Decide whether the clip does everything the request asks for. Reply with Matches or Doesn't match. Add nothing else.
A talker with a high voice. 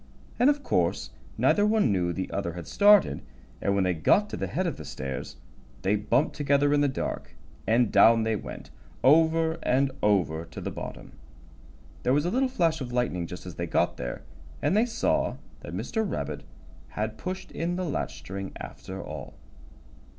Doesn't match